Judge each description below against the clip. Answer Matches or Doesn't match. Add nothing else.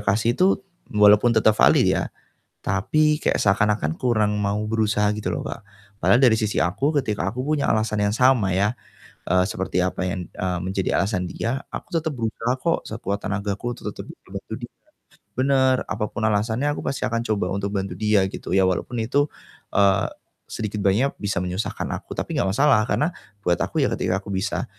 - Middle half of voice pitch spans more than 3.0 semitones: Matches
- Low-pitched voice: Matches